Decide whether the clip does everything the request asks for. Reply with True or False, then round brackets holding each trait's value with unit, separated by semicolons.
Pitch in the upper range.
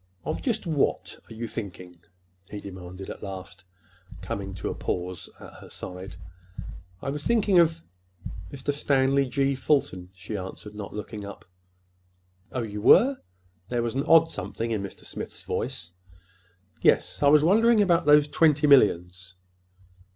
False (115 Hz)